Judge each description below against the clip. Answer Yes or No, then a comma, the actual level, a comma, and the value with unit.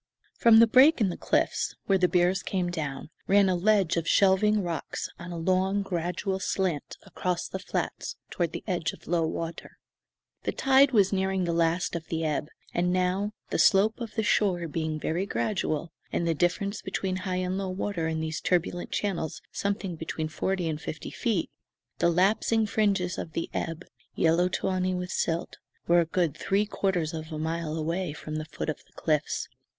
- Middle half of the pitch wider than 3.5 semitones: No, average, 3.0 semitones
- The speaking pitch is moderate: Yes, medium, 180 Hz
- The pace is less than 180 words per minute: No, average, 185 wpm